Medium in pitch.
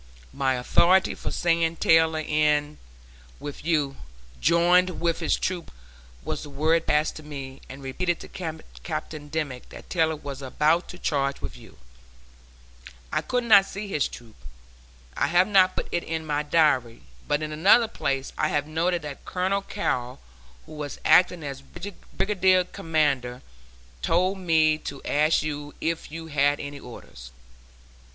Yes: medium, 155 Hz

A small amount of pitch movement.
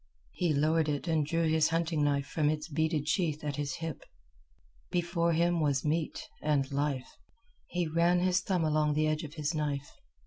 Yes: narrow, 2.2 semitones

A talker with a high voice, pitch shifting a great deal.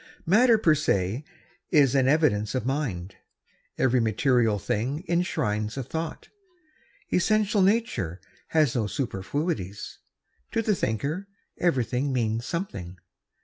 No: low, 135 Hz; wide, 7.5 semitones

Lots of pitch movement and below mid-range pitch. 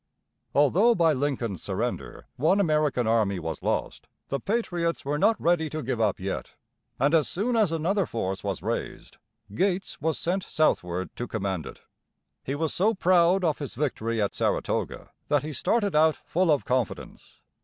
No: wide, 7.2 semitones; medium, 150 Hz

